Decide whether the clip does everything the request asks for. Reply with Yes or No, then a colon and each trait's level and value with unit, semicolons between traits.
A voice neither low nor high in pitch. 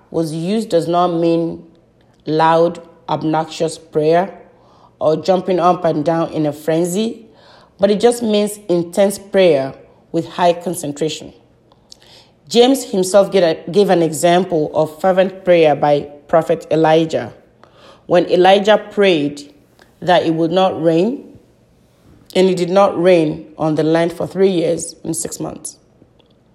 Yes: medium, 170 Hz